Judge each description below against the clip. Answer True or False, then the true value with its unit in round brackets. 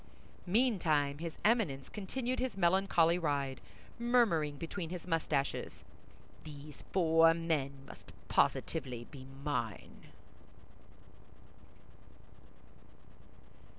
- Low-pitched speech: False (165 Hz)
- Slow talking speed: True (80 wpm)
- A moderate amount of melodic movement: True (5.0 semitones)